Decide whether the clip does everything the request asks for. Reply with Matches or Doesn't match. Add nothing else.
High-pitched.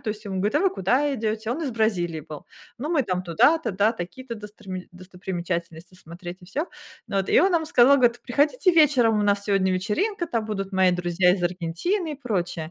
Matches